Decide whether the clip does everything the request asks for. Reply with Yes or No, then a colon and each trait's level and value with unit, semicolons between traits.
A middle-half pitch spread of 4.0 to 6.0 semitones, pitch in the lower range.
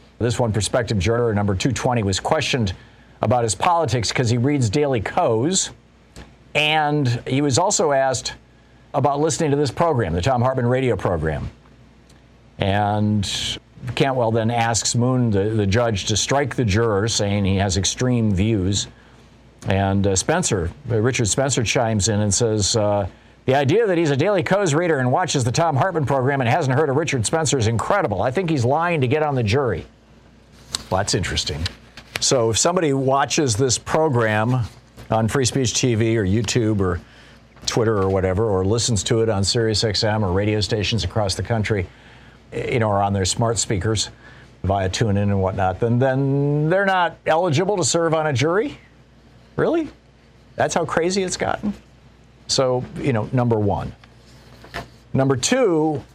Yes: average, 4.6 semitones; low, 120 Hz